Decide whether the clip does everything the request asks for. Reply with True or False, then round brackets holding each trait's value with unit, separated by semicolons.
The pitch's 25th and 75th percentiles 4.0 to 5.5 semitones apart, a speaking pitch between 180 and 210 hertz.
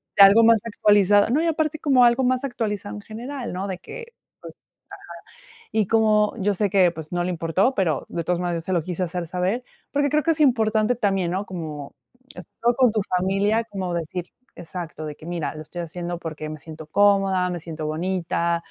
True (4.6 semitones; 190 Hz)